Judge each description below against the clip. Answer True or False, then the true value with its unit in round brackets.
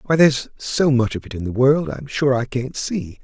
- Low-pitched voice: True (130 Hz)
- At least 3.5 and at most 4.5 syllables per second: False (5.1 syllables/s)